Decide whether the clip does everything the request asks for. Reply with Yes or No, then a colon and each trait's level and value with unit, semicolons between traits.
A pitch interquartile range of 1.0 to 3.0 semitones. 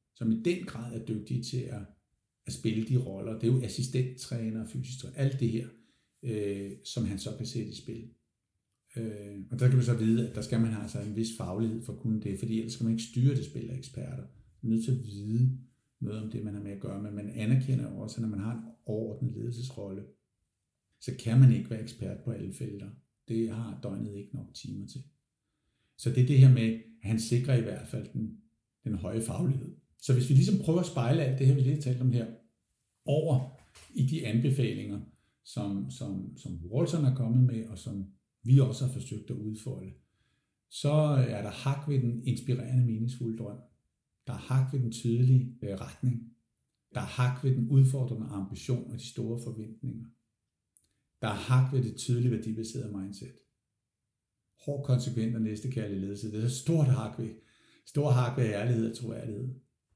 Yes: narrow, 2.6 semitones